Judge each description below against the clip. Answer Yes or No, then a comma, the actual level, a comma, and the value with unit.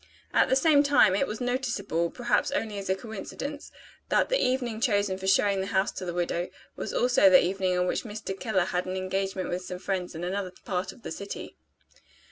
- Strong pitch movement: No, average, 4.3 semitones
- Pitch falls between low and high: No, high, 195 Hz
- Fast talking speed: Yes, fast, 210 wpm